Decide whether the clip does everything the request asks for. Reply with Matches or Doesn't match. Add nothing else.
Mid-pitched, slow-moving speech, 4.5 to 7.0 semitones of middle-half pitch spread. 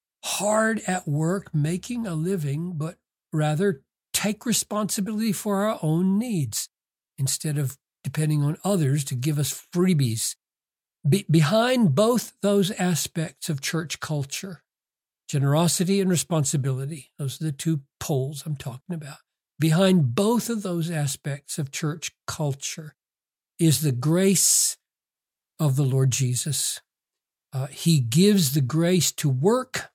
Matches